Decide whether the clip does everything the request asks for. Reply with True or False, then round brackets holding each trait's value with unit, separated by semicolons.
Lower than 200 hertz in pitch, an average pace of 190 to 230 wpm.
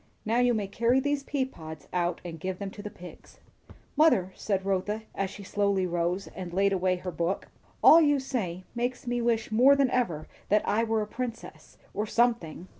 False (205 Hz; 195 wpm)